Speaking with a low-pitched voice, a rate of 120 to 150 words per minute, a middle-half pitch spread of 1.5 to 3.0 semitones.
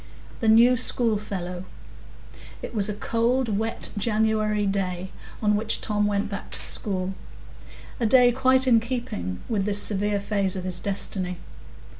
No: high, 210 Hz; average, 145 wpm; average, 2.7 semitones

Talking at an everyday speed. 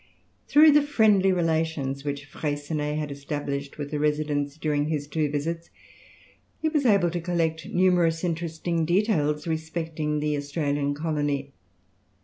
No: slow, 130 wpm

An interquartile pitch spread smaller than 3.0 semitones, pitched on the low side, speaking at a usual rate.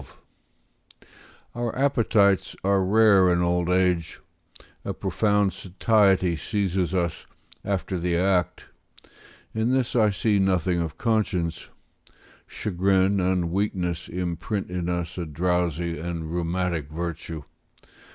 No: narrow, 2.5 semitones; very low, 90 Hz; slow, 110 wpm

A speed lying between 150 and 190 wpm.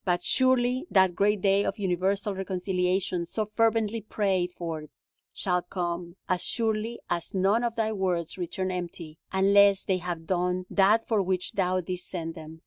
Yes: average, 160 wpm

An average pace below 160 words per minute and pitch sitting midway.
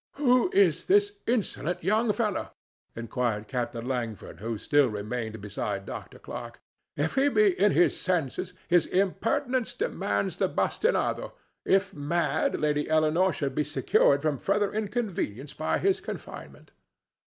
Yes: slow, 135 wpm; medium, 165 Hz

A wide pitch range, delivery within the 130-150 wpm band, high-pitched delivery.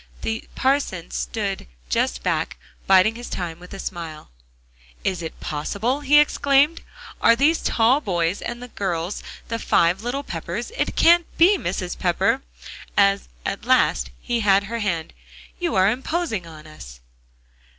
Yes: wide, 6.8 semitones; average, 145 wpm; high, 200 Hz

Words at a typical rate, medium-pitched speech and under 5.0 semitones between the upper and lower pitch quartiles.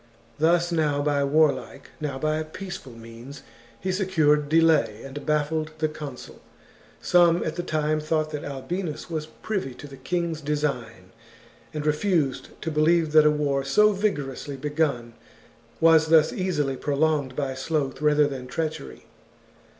Yes: average, 160 wpm; medium, 150 Hz; average, 2.7 semitones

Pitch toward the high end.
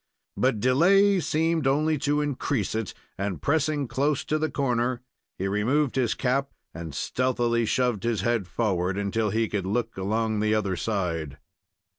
No: low, 120 Hz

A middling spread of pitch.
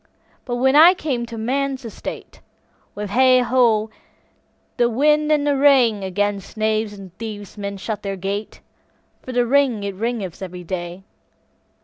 Yes: average, 4.4 semitones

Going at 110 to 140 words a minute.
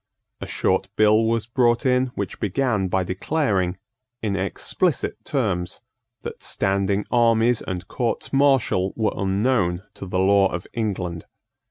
Yes: slow, 135 wpm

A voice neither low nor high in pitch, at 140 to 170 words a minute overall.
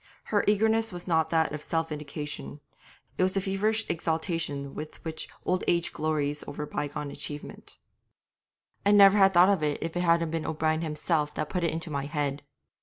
No: medium, 160 Hz; average, 180 wpm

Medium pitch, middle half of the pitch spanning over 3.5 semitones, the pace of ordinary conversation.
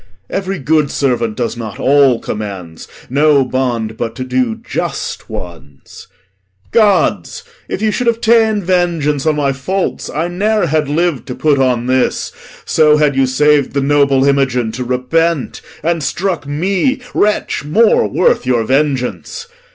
Yes: medium, 145 Hz; average, 5.2 semitones; average, 150 wpm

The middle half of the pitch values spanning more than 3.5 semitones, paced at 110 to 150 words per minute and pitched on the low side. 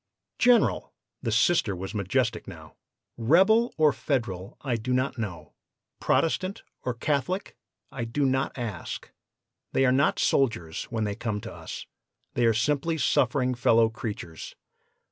Yes: average, 4.5 semitones; average, 140 wpm; low, 120 Hz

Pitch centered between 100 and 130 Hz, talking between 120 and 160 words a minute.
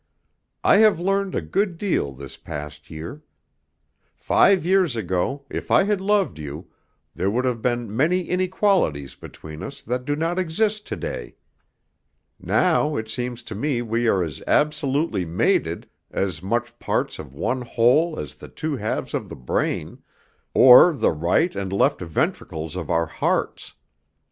Yes: low, 125 Hz; average, 155 wpm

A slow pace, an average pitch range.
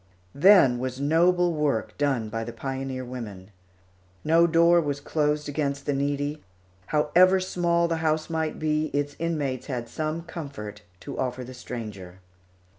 No: average, 145 wpm; average, 4.1 semitones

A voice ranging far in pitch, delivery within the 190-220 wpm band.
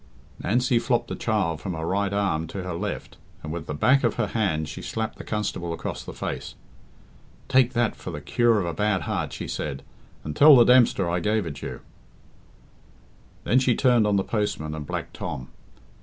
Yes: wide, 6.0 semitones; average, 200 wpm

